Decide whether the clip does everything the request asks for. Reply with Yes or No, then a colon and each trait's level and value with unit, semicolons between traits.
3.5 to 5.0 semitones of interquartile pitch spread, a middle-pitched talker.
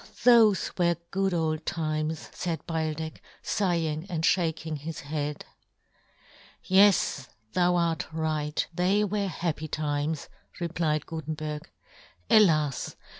No: narrow, 2.5 semitones; medium, 160 Hz